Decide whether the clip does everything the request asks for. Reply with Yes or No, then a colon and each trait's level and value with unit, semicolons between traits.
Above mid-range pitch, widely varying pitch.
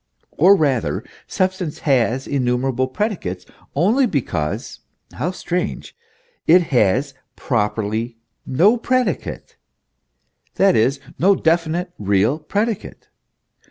No: medium, 145 Hz; wide, 7.3 semitones